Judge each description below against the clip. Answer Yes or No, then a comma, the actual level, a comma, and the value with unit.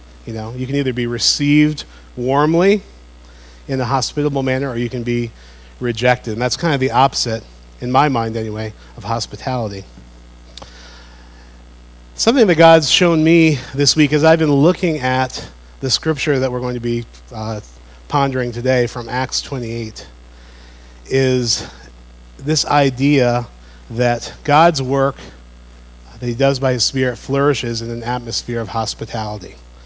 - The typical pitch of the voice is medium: No, low, 120 Hz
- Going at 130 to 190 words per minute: Yes, average, 145 wpm